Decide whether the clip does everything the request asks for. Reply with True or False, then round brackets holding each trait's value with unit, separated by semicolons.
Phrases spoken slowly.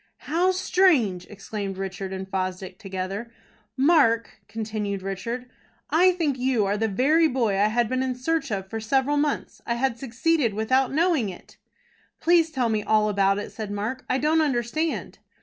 False (165 wpm)